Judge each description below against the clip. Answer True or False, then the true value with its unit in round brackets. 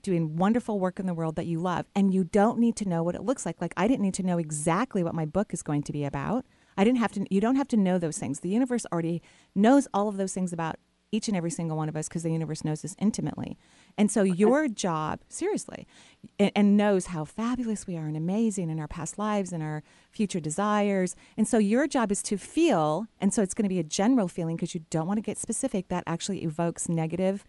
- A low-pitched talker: False (190 Hz)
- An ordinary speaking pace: False (255 wpm)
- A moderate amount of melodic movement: True (4.3 semitones)